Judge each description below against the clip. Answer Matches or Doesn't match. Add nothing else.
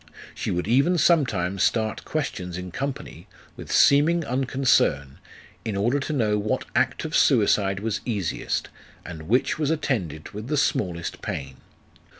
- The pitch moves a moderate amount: Doesn't match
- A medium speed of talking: Matches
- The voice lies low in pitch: Matches